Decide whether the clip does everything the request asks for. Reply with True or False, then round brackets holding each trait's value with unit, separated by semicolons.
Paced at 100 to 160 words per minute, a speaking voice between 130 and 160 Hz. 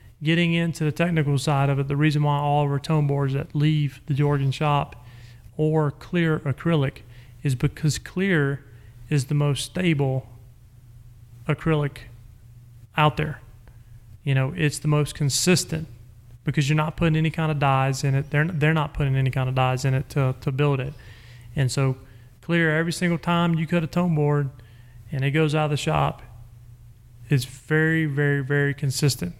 False (175 wpm; 140 Hz)